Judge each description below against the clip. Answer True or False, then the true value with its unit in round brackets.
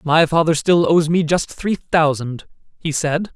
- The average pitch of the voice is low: False (160 Hz)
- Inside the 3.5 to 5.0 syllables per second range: True (4.1 syllables/s)